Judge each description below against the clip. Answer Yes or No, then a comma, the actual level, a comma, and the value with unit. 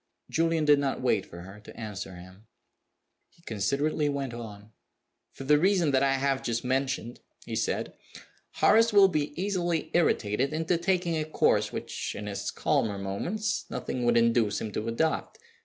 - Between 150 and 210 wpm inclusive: Yes, average, 165 wpm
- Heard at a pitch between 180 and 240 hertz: No, low, 135 Hz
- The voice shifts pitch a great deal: Yes, wide, 6.8 semitones